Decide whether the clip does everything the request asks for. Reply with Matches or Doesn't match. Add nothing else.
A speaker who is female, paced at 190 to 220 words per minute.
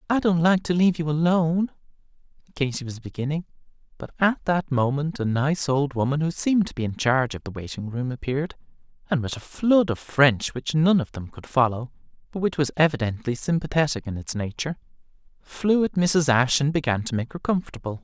Doesn't match